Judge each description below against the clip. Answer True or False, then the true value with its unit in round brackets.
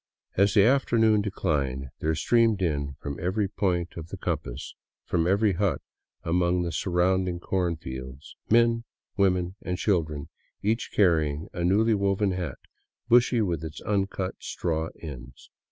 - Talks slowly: False (150 wpm)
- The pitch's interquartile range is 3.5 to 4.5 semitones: True (4.0 semitones)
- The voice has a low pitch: True (90 Hz)